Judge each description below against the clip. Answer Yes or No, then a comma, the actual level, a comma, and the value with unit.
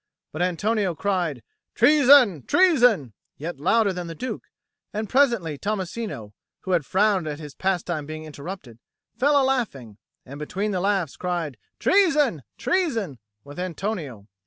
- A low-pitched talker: No, medium, 185 Hz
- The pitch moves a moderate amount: No, wide, 6.7 semitones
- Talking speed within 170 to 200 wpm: No, slow, 135 wpm